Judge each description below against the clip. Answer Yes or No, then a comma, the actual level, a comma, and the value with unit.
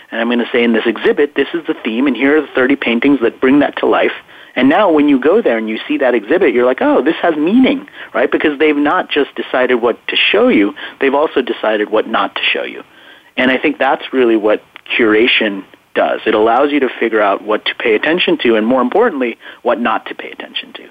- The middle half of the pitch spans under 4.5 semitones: No, average, 5.2 semitones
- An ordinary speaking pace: No, fast, 245 wpm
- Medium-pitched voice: No, low, 130 Hz